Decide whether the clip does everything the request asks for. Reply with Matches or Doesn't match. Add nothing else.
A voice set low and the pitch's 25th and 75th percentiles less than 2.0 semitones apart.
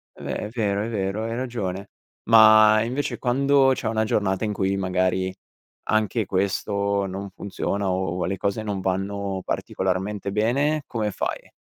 Doesn't match